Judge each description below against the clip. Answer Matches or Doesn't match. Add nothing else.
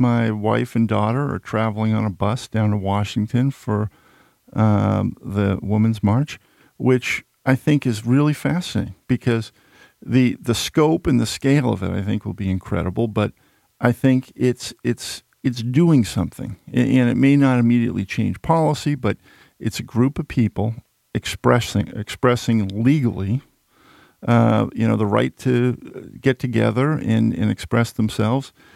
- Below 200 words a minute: Matches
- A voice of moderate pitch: Doesn't match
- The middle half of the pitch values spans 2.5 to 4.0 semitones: Matches